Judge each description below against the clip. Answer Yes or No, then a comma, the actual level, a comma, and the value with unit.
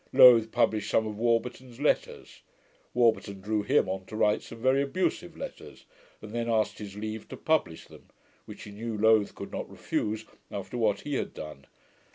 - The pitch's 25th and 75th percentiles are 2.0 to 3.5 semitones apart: Yes, narrow, 2.4 semitones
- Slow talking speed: No, average, 180 wpm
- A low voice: Yes, low, 110 Hz